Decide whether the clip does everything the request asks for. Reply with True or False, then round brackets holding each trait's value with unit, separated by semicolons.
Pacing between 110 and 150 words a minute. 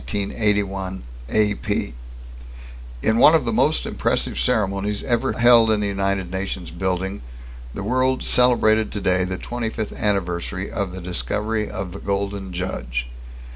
True (140 wpm)